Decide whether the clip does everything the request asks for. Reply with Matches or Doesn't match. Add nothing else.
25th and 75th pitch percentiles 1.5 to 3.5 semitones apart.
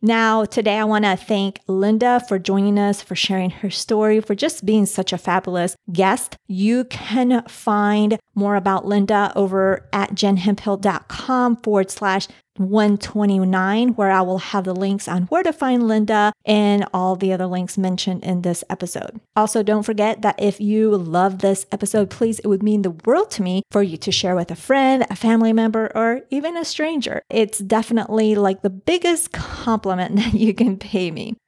Matches